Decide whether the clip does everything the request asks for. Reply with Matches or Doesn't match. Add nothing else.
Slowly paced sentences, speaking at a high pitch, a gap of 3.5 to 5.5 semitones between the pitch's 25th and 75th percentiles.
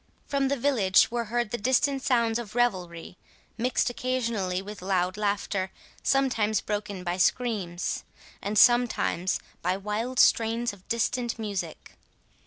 Matches